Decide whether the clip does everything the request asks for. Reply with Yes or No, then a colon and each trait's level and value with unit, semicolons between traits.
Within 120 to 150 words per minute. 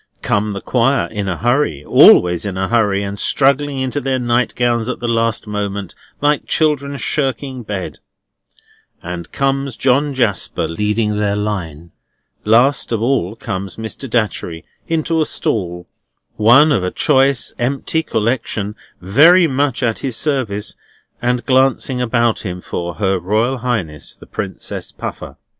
Yes: average, 145 wpm